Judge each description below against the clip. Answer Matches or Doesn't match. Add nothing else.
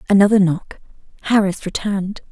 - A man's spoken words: Doesn't match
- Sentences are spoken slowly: Matches